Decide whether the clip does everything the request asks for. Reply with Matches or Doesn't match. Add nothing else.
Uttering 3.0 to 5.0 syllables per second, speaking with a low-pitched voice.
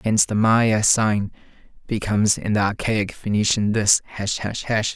Matches